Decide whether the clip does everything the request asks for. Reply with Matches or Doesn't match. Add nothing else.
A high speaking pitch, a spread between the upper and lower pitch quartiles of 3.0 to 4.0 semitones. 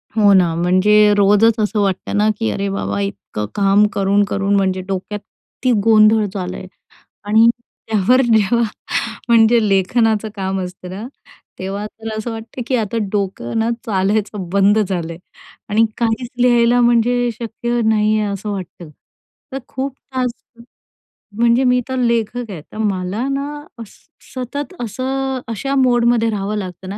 Matches